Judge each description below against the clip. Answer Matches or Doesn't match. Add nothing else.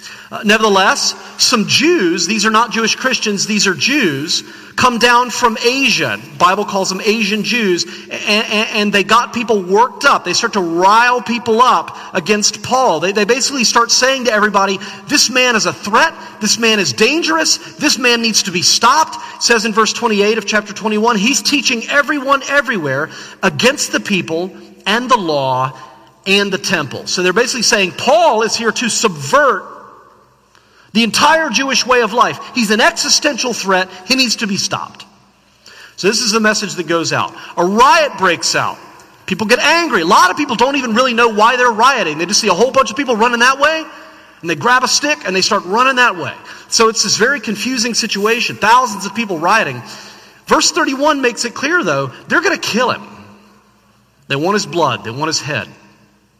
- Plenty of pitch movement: Doesn't match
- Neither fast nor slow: Matches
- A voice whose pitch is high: Matches